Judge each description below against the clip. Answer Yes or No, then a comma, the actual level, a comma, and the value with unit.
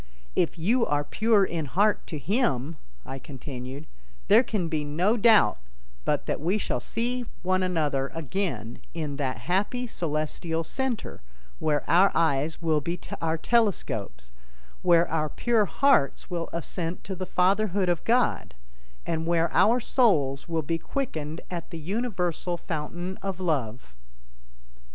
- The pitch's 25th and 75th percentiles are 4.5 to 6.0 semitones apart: Yes, average, 4.8 semitones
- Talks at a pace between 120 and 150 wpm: Yes, average, 140 wpm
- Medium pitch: Yes, medium, 170 Hz